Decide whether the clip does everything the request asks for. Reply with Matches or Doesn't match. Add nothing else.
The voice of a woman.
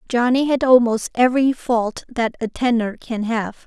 Matches